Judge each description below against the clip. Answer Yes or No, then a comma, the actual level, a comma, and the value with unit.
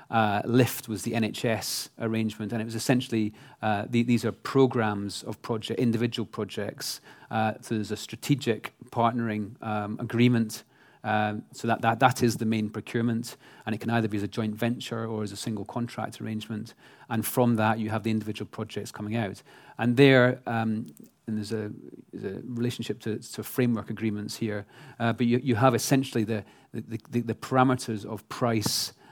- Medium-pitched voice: No, low, 115 Hz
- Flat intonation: Yes, narrow, 1.8 semitones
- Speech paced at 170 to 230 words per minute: Yes, average, 180 wpm